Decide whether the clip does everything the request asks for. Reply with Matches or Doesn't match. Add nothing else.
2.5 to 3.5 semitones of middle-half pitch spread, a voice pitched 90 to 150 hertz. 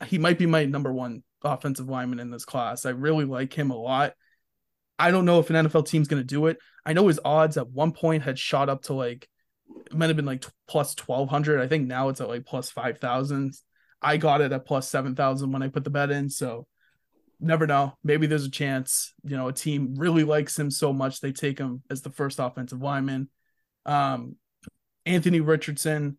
Matches